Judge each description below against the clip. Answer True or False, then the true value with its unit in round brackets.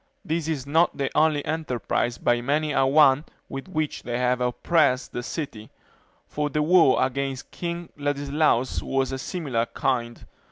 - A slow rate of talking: False (160 wpm)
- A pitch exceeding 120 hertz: True (140 Hz)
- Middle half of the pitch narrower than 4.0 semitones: True (3.5 semitones)